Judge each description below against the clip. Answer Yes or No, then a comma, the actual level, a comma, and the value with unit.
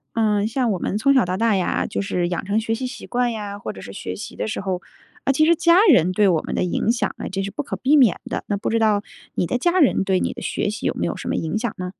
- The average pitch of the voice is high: Yes, high, 210 Hz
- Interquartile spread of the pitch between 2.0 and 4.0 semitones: No, average, 4.7 semitones